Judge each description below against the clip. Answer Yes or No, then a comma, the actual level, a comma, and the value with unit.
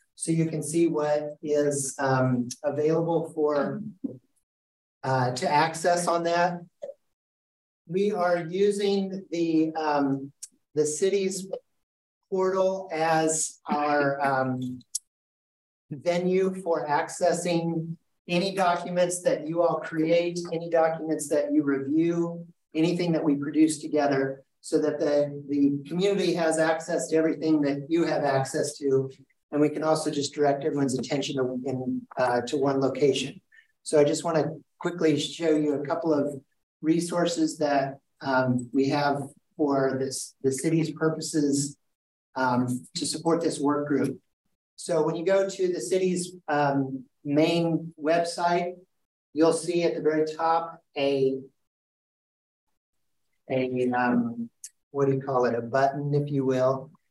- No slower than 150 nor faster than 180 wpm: No, slow, 135 wpm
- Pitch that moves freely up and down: No, average, 3.4 semitones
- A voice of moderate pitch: Yes, medium, 155 Hz